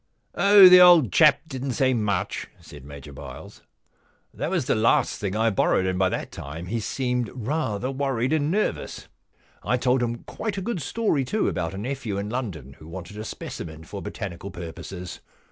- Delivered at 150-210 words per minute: Yes, average, 185 wpm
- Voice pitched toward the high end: No, low, 115 Hz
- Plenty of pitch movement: Yes, wide, 6.8 semitones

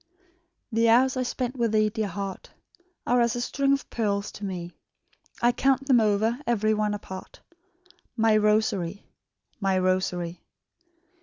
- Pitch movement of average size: Yes, average, 3.2 semitones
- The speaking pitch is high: Yes, high, 215 Hz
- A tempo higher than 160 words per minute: No, average, 145 wpm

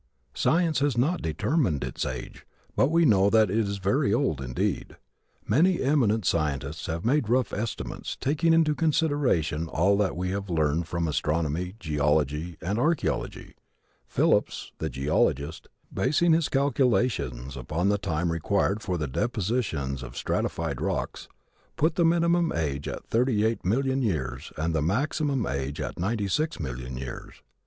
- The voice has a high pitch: No, low, 100 Hz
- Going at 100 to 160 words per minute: Yes, average, 150 wpm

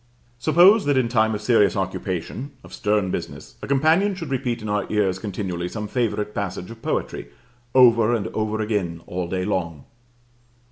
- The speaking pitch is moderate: No, low, 105 Hz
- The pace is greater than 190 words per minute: No, average, 170 wpm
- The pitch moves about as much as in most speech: Yes, average, 4.6 semitones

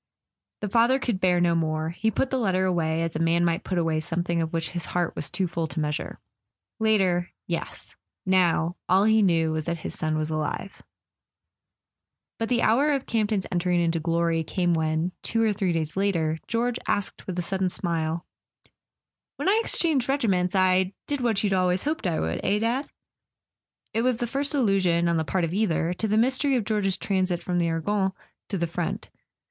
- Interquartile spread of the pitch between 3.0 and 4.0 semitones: No, average, 4.4 semitones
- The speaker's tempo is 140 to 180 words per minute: No, average, 195 wpm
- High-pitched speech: No, medium, 180 Hz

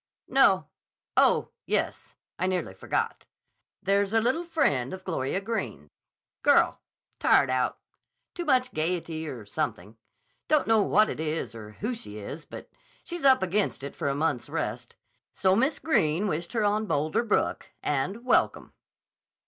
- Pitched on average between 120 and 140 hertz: No, medium, 185 Hz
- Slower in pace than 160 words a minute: Yes, average, 150 wpm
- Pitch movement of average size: No, wide, 7.9 semitones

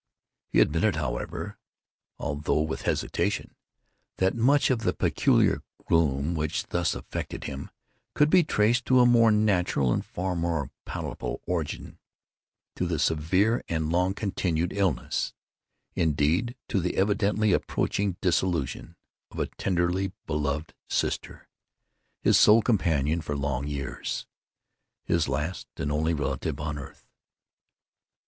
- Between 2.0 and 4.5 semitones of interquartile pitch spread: No, average, 4.9 semitones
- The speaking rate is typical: No, slow, 115 wpm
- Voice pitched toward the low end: Yes, very low, 85 Hz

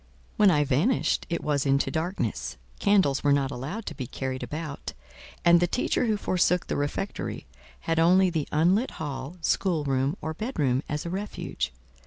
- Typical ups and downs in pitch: Yes, average, 4.7 semitones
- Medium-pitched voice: Yes, medium, 160 Hz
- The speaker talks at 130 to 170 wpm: Yes, average, 160 wpm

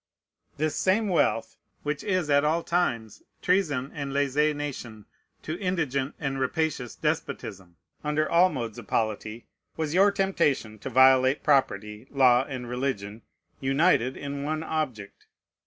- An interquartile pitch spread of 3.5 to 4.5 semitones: Yes, average, 4.2 semitones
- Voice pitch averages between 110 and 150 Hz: Yes, medium, 140 Hz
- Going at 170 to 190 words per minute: No, average, 140 wpm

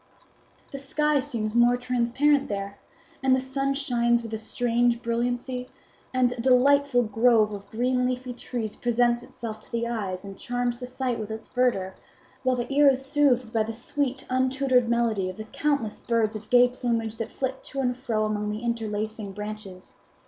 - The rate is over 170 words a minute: Yes, average, 180 wpm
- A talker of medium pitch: No, high, 240 Hz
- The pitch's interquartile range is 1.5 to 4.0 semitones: Yes, average, 2.7 semitones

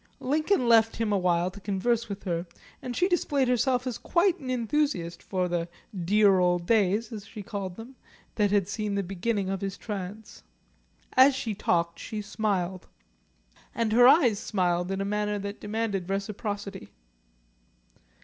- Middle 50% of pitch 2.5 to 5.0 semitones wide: Yes, average, 3.6 semitones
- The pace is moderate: Yes, average, 160 wpm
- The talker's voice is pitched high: Yes, high, 205 Hz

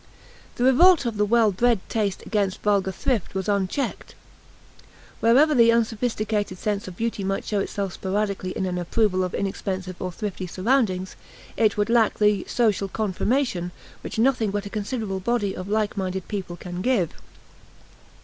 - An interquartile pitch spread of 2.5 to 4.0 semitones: Yes, average, 3.3 semitones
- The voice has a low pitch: No, high, 205 Hz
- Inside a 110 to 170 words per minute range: Yes, average, 160 wpm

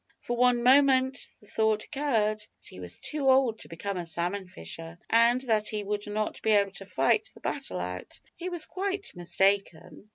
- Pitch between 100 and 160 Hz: No, high, 215 Hz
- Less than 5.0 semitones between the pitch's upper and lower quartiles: No, wide, 5.4 semitones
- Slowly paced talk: No, average, 190 wpm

